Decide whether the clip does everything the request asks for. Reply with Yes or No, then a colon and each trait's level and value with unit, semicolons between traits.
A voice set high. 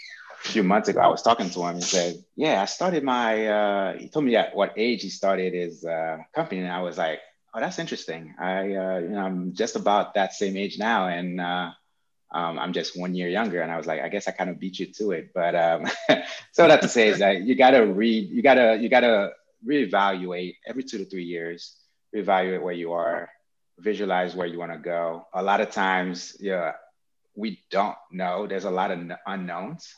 No: very low, 90 Hz